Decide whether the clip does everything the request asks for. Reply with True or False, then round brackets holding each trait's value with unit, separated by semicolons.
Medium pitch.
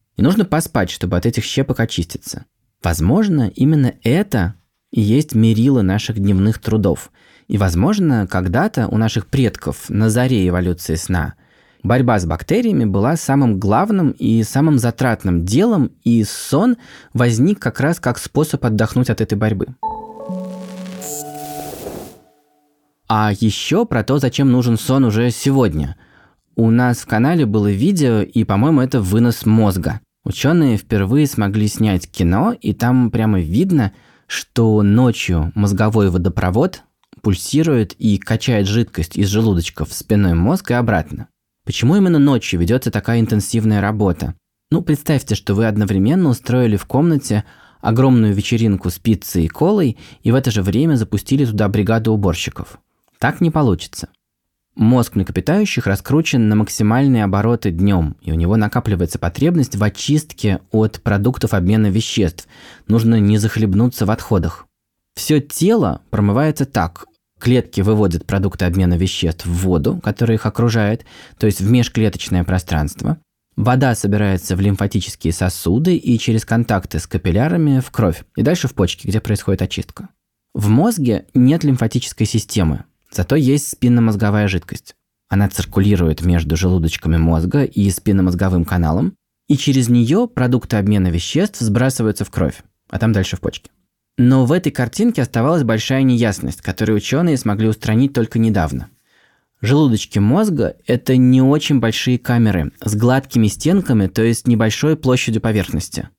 False (110 Hz)